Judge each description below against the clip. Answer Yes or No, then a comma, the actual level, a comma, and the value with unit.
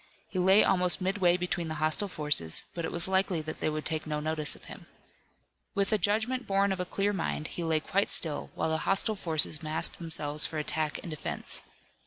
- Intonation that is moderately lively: Yes, average, 3.7 semitones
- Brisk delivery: Yes, fast, 210 wpm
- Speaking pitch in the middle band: Yes, medium, 170 Hz